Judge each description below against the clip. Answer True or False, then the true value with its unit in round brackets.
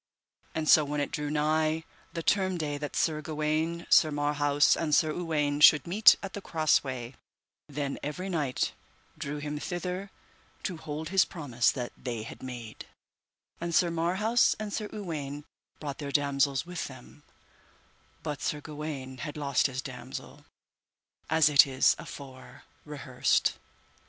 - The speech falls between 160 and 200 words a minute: False (150 wpm)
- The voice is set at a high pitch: False (150 Hz)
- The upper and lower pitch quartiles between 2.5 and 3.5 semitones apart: True (2.8 semitones)